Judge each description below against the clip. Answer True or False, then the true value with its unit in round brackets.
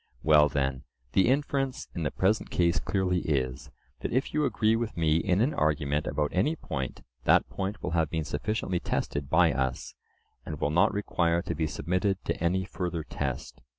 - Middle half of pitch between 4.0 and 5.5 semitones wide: True (4.5 semitones)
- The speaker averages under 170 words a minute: False (185 wpm)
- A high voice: False (85 Hz)